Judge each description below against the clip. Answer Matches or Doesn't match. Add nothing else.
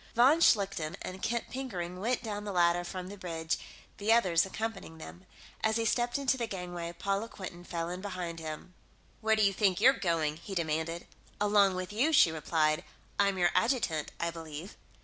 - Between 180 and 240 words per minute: Matches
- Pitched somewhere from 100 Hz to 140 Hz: Doesn't match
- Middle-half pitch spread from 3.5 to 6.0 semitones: Matches